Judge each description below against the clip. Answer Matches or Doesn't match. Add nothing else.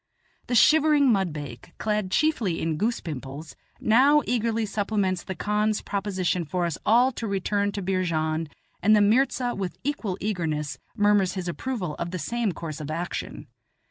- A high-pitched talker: Matches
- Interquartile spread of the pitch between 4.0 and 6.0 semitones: Matches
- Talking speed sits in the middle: Matches